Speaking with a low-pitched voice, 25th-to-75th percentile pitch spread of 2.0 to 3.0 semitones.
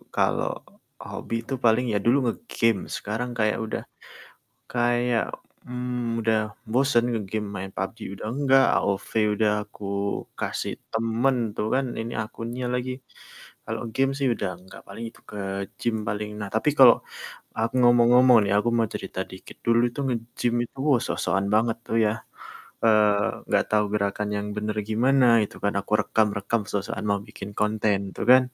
Yes: low, 115 Hz; average, 2.7 semitones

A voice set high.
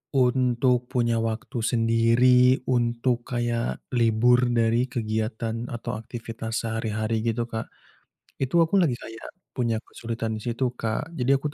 No: low, 120 Hz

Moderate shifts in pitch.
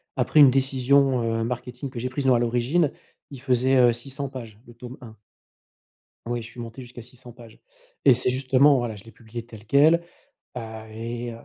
No: narrow, 2.3 semitones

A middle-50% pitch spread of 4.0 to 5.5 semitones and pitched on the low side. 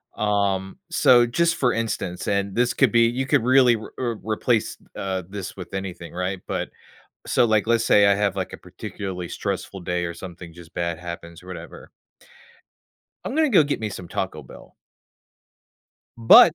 Yes: average, 4.6 semitones; low, 100 Hz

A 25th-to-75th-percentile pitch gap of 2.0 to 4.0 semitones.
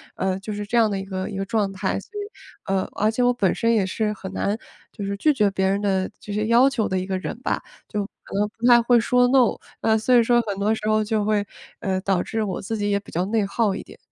Yes: average, 2.7 semitones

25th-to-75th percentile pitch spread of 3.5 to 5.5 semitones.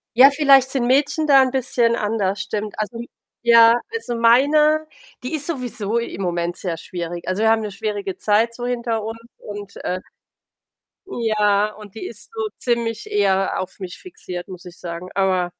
Yes: average, 4.1 semitones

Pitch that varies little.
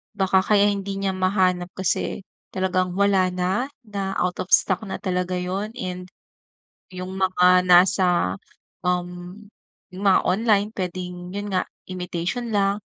Yes: narrow, 1.5 semitones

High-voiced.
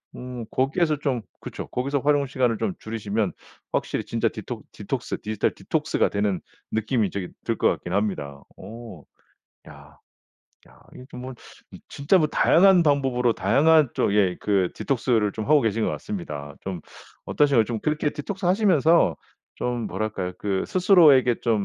No: low, 120 Hz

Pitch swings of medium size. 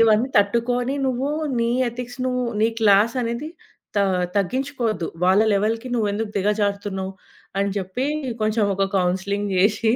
Yes: average, 3.4 semitones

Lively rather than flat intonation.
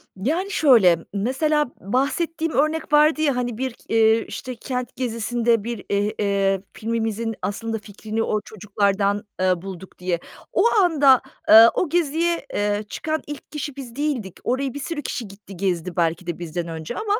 Yes: wide, 6.3 semitones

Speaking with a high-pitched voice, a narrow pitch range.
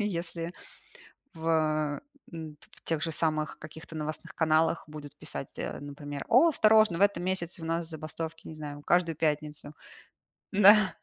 No: medium, 160 Hz; narrow, 2.0 semitones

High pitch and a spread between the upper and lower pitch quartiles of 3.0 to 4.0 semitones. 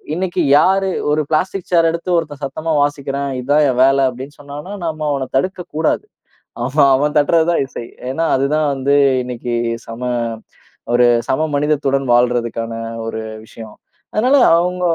No: medium, 145 Hz; average, 3.7 semitones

